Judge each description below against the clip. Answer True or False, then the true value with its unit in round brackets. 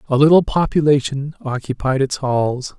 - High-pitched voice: False (140 Hz)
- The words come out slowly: True (130 wpm)